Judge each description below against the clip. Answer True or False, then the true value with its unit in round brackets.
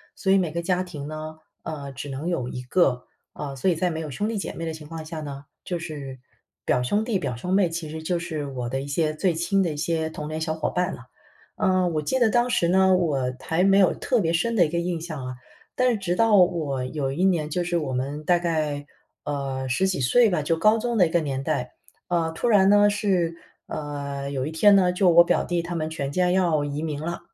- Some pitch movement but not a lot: True (3.9 semitones)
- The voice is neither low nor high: True (165 Hz)